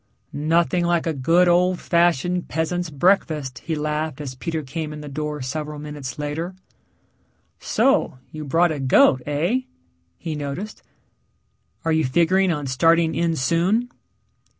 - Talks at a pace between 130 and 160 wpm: Yes, average, 140 wpm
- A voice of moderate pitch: Yes, medium, 160 Hz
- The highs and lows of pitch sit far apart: No, average, 2.8 semitones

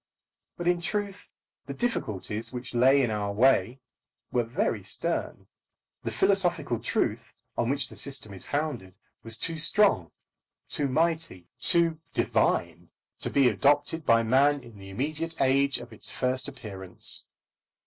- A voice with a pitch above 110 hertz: Yes, low, 135 Hz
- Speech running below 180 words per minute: Yes, average, 140 wpm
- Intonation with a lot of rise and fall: Yes, wide, 5.9 semitones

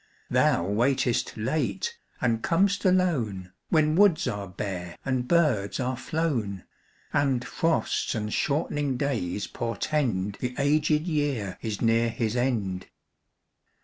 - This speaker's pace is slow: Yes, slow, 115 wpm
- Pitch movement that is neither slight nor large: No, wide, 6.6 semitones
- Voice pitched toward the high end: No, low, 125 Hz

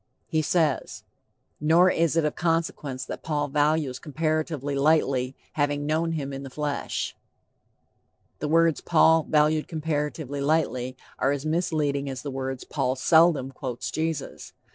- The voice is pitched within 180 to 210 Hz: No, medium, 150 Hz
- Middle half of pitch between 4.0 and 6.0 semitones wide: No, narrow, 2.6 semitones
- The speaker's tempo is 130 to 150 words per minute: Yes, average, 140 wpm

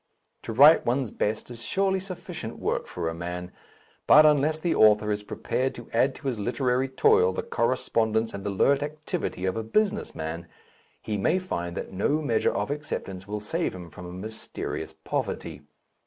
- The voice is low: Yes, low, 115 Hz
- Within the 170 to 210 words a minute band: Yes, average, 175 wpm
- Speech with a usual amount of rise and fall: No, wide, 7.2 semitones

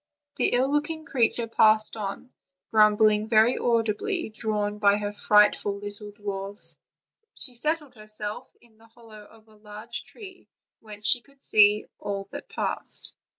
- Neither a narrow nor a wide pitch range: No, narrow, 2.3 semitones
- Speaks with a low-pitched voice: No, high, 215 Hz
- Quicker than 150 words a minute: No, average, 145 wpm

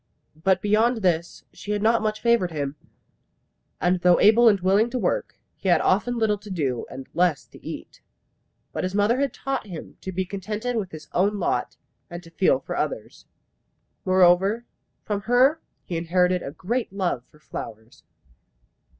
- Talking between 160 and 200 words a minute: Yes, average, 170 wpm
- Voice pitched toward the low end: No, high, 190 Hz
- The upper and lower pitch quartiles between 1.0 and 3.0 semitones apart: No, average, 3.9 semitones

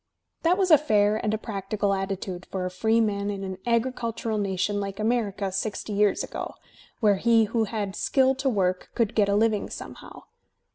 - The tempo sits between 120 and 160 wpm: No, average, 180 wpm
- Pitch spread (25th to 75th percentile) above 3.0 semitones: No, narrow, 2.5 semitones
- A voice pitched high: Yes, high, 210 Hz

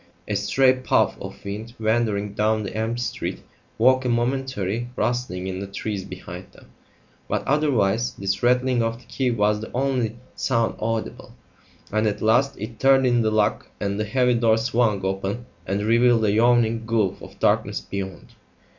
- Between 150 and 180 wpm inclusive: Yes, average, 170 wpm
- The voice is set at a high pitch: No, low, 115 Hz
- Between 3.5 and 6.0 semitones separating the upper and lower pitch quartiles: No, average, 2.9 semitones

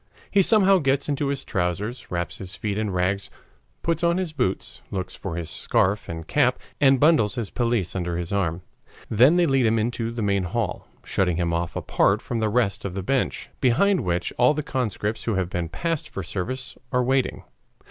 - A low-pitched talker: Yes, low, 110 Hz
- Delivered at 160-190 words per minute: No, average, 200 wpm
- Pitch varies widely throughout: Yes, wide, 6.4 semitones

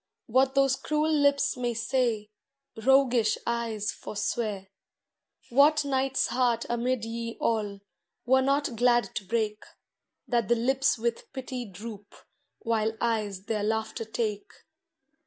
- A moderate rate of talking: No, slow, 120 wpm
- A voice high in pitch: Yes, high, 235 Hz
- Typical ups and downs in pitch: Yes, average, 3.2 semitones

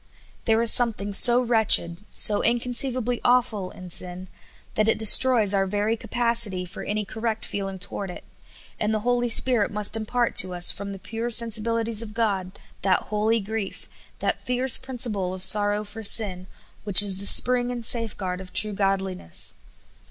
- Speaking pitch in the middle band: No, high, 215 Hz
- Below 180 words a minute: Yes, average, 165 wpm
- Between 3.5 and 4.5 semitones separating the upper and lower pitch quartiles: No, average, 3.1 semitones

